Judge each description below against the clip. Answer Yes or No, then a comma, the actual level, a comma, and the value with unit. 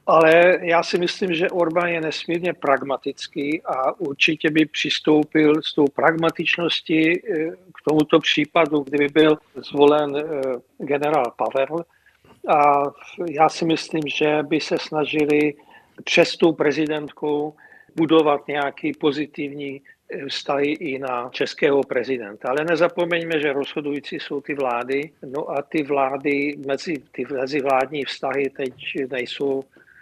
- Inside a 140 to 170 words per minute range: No, average, 120 wpm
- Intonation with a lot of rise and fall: No, narrow, 2.4 semitones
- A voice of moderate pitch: Yes, medium, 150 Hz